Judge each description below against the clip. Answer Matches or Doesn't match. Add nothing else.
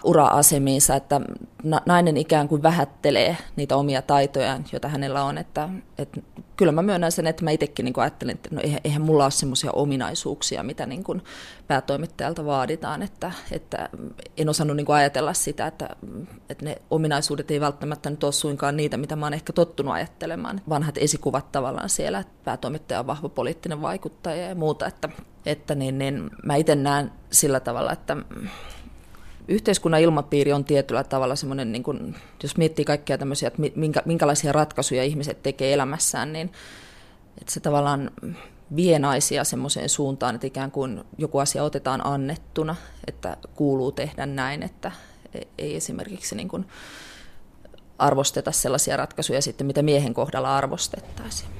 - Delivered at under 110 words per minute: Doesn't match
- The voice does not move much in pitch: Matches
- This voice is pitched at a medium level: Matches